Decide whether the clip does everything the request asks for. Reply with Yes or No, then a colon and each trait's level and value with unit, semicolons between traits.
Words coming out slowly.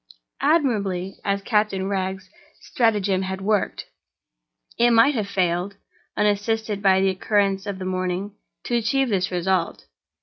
Yes: slow, 115 wpm